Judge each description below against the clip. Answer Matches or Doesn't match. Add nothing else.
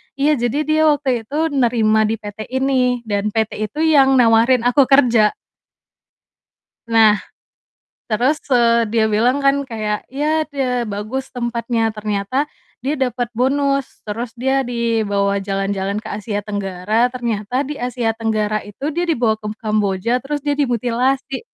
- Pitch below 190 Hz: Doesn't match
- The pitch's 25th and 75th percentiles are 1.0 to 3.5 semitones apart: Doesn't match